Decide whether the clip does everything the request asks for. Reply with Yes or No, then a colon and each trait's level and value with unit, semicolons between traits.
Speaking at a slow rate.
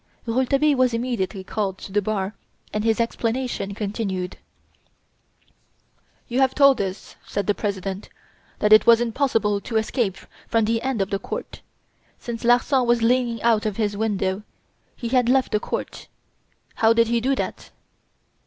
No: average, 155 wpm